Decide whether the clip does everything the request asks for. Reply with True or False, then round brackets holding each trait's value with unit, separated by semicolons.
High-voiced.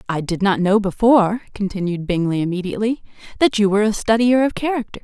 True (205 Hz)